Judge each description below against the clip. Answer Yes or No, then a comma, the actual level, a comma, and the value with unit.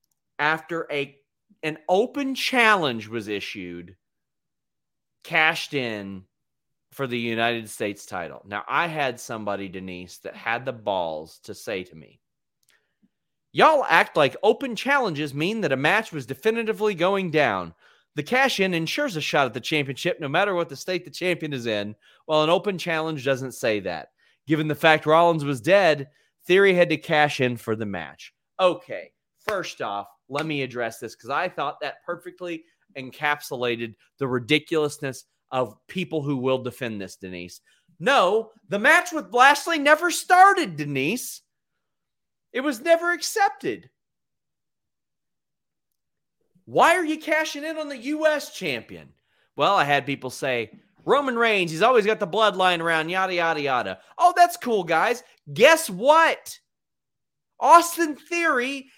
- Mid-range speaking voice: Yes, medium, 160 Hz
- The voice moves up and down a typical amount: No, wide, 8.8 semitones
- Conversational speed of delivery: Yes, average, 150 wpm